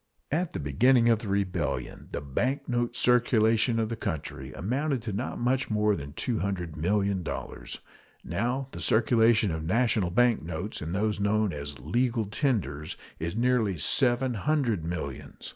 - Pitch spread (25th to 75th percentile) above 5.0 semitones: Yes, wide, 5.6 semitones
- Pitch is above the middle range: No, low, 110 Hz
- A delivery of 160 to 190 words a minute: No, average, 145 wpm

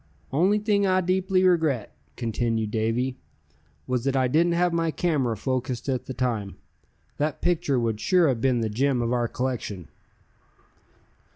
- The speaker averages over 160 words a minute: No, average, 155 wpm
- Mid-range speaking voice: No, low, 130 Hz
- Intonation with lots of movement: Yes, wide, 6.3 semitones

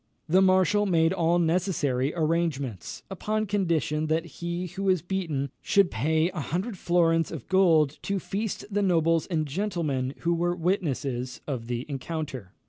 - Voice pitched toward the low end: No, medium, 165 Hz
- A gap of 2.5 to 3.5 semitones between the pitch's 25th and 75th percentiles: No, average, 4.0 semitones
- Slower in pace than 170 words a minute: Yes, average, 150 wpm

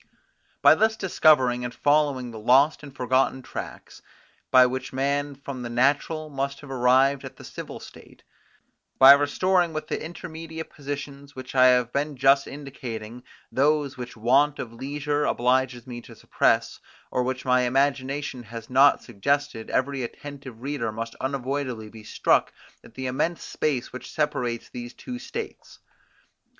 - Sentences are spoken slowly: No, average, 150 wpm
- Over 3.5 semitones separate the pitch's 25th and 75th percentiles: No, narrow, 2.5 semitones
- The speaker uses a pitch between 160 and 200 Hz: No, low, 135 Hz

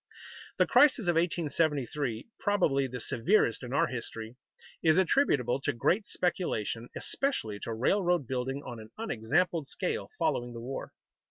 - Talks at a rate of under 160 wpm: Yes, average, 140 wpm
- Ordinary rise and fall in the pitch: No, wide, 6.6 semitones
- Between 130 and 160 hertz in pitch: Yes, medium, 140 Hz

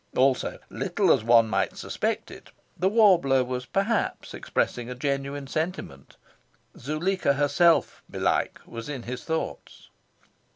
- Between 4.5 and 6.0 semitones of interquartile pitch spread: Yes, average, 5.2 semitones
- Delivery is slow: Yes, slow, 125 wpm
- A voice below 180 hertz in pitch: Yes, medium, 140 Hz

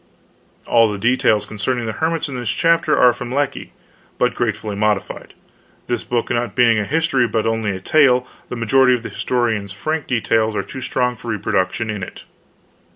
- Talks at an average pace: Yes, average, 185 wpm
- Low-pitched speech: Yes, low, 120 Hz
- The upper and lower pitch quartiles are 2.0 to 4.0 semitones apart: Yes, average, 2.9 semitones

